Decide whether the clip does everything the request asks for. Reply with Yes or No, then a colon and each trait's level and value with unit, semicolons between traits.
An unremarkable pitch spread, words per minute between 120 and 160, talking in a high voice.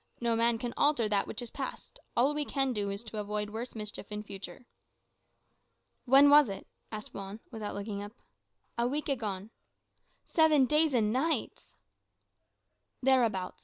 Yes: average, 4.4 semitones; average, 155 wpm; high, 230 Hz